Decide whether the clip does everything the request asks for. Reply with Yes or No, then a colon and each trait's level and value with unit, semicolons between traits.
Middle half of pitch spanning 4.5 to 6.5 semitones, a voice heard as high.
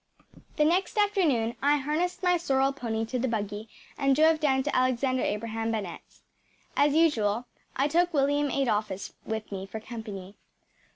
Yes: average, 5.0 semitones; very high, 260 Hz